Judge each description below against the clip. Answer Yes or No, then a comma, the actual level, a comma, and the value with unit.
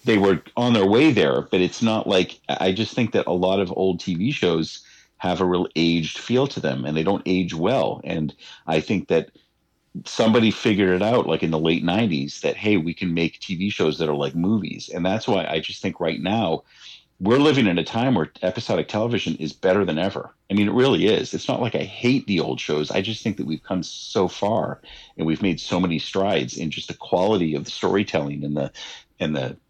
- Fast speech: Yes, fast, 230 wpm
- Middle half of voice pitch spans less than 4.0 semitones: No, average, 4.7 semitones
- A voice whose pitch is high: No, very low, 90 Hz